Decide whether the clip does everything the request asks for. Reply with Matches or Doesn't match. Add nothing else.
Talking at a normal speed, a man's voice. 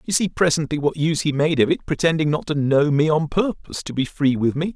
Doesn't match